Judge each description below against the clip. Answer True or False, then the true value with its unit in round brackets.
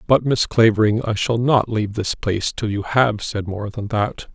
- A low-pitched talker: True (110 Hz)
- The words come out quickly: True (220 wpm)